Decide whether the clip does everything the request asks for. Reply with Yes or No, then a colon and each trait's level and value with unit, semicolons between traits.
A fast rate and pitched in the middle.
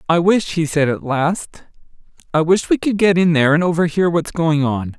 Yes: fast, 215 wpm; medium, 165 Hz